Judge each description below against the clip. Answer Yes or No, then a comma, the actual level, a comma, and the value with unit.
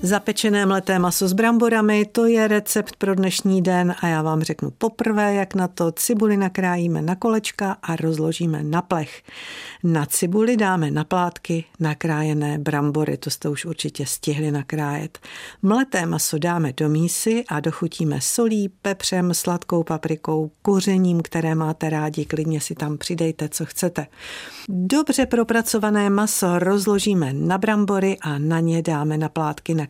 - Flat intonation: No, average, 4.5 semitones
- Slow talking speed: No, average, 145 wpm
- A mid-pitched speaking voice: Yes, medium, 175 Hz